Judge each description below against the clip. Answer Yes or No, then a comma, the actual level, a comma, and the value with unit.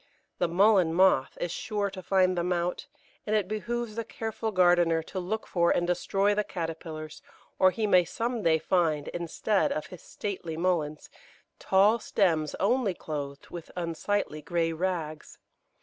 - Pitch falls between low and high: Yes, medium, 180 Hz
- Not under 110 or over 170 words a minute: Yes, average, 155 wpm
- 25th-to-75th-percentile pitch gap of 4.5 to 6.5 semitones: No, average, 3.8 semitones